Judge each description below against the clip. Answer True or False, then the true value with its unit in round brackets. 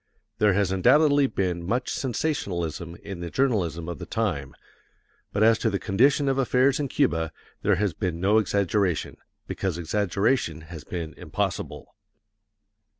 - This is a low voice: True (100 Hz)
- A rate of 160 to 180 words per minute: False (145 wpm)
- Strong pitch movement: True (6.1 semitones)